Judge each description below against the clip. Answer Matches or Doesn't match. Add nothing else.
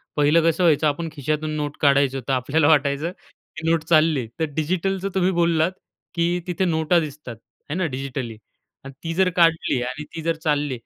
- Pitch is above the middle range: Doesn't match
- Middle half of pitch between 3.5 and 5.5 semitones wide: Doesn't match